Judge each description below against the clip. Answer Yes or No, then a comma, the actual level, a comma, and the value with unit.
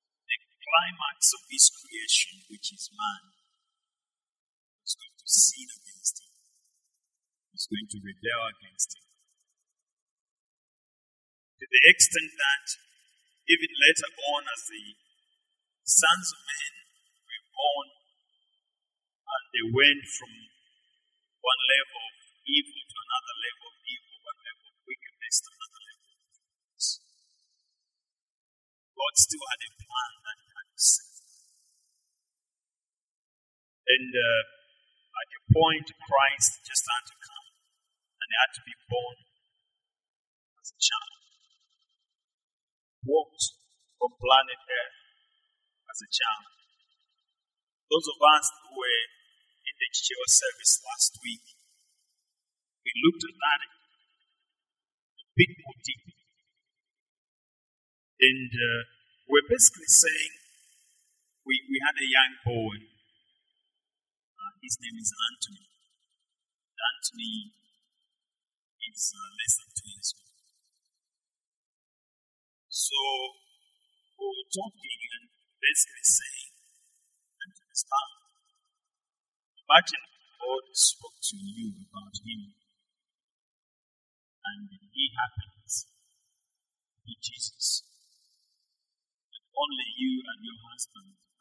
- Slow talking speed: Yes, slow, 105 wpm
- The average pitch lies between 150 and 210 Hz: No, very high, 325 Hz